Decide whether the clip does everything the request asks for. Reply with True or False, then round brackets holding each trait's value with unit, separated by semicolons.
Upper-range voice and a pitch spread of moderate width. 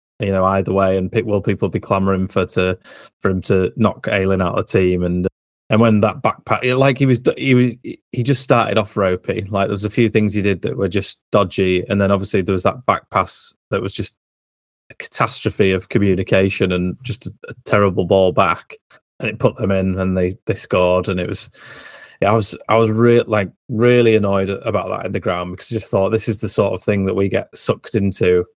False (100 Hz; 3.0 semitones)